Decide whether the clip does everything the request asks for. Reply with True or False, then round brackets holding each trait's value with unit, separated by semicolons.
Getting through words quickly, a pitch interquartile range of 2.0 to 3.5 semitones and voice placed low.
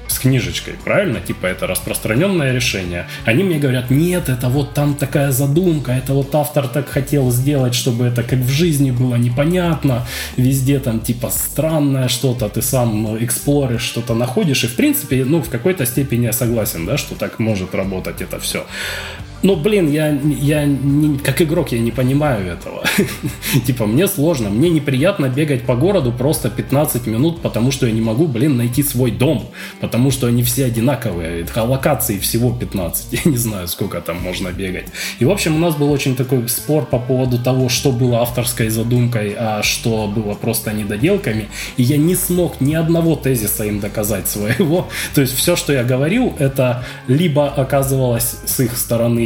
False (180 wpm; 4.0 semitones; 130 Hz)